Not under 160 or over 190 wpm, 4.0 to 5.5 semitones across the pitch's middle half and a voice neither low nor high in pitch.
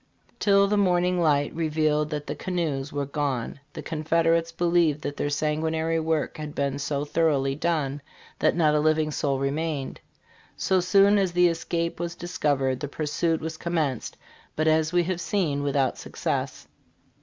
No: average, 165 wpm; average, 2.8 semitones; medium, 155 Hz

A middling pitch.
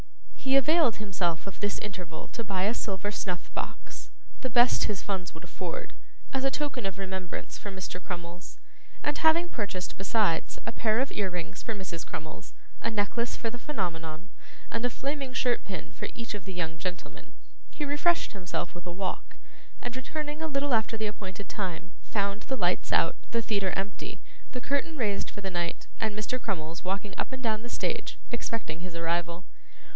No: high, 205 Hz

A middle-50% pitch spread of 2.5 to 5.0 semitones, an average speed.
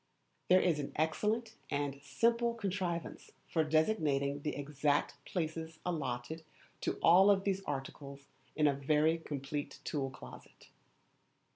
No: average, 4.3 semitones; slow, 120 wpm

